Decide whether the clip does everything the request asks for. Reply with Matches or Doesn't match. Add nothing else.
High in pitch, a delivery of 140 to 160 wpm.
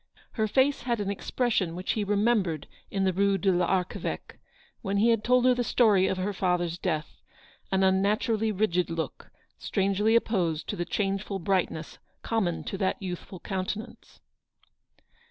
Matches